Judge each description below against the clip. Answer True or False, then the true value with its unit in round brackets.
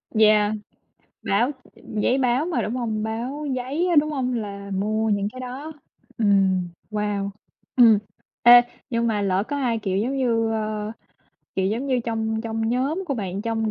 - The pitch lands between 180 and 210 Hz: False (225 Hz)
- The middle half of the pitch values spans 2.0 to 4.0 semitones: True (3.3 semitones)